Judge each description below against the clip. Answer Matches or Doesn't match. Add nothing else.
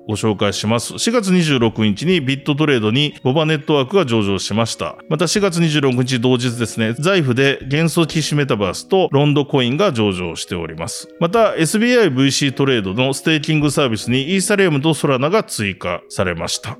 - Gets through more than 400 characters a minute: Doesn't match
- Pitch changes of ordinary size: Doesn't match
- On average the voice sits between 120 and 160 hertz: Matches